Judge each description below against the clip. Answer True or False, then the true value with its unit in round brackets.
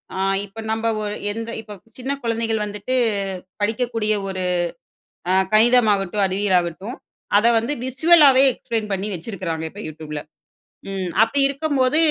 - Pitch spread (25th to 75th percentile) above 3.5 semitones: True (3.9 semitones)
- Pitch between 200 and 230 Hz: True (215 Hz)